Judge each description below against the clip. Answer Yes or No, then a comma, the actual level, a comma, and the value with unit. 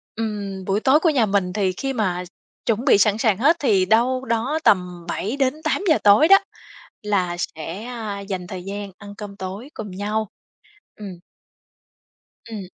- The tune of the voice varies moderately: Yes, average, 4.1 semitones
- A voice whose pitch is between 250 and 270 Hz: No, high, 210 Hz